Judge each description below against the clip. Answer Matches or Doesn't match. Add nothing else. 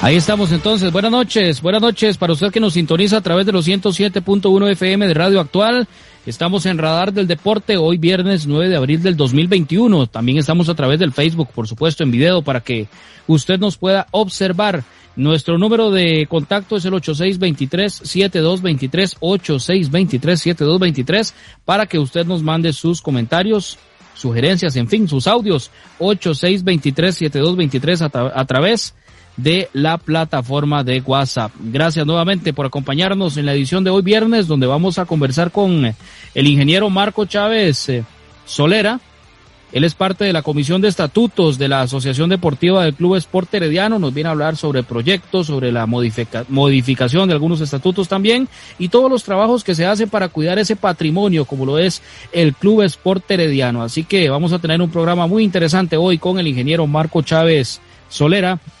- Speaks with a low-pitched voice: Doesn't match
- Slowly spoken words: Doesn't match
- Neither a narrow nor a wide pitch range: Matches